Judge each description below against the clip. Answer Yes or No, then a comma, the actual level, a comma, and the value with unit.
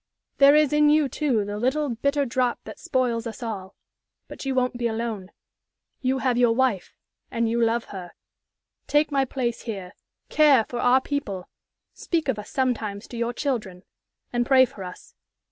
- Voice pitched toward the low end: No, high, 240 Hz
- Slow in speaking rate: No, average, 175 wpm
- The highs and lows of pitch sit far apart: No, average, 3.3 semitones